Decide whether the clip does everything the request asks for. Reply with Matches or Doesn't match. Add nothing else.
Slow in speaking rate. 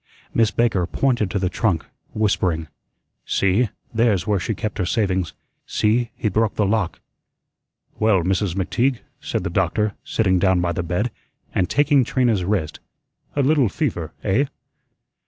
Doesn't match